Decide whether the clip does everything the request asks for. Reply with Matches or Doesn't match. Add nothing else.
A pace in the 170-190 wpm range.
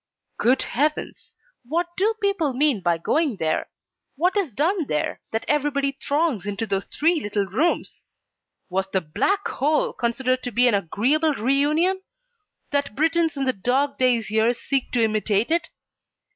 Doesn't match